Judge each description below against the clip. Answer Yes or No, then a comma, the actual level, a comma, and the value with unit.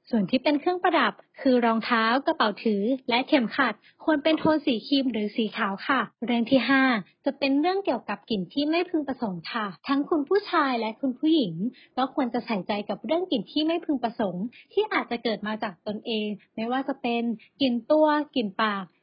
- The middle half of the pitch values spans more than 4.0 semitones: Yes, average, 5.1 semitones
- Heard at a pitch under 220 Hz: No, very high, 250 Hz